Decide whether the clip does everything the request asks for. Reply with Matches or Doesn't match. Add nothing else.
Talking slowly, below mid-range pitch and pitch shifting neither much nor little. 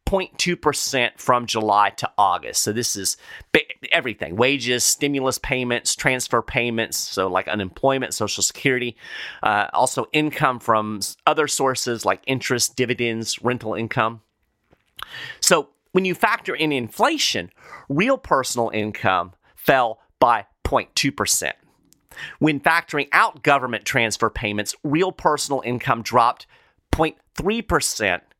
Matches